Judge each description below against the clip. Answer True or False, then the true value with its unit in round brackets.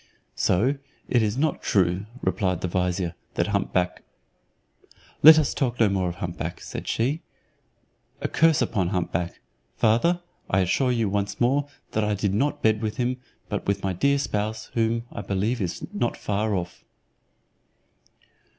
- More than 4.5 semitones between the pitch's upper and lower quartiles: True (5.1 semitones)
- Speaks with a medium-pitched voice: False (105 Hz)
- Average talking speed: True (170 wpm)